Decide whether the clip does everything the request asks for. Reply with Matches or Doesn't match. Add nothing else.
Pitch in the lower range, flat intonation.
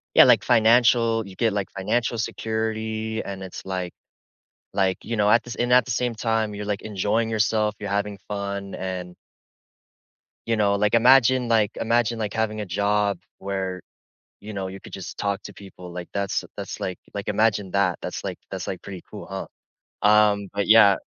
Matches